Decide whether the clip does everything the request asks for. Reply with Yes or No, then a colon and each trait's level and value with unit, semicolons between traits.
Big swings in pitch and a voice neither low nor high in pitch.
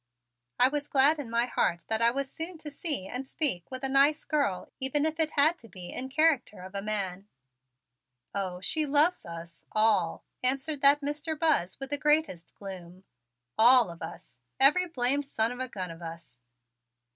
No: wide, 7.6 semitones; very high, 255 Hz